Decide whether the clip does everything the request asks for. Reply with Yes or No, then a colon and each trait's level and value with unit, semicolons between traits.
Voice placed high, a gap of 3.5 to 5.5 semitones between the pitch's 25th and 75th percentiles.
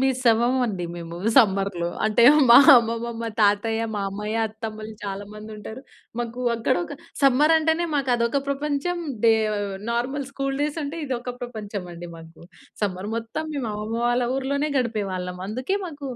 Yes: high, 230 Hz; average, 4.4 semitones